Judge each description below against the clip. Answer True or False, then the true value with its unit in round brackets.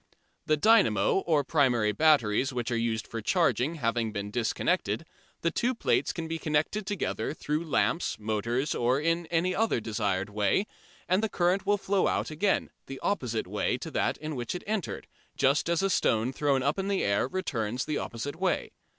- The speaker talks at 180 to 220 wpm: True (185 wpm)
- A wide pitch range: True (7.2 semitones)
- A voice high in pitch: False (145 Hz)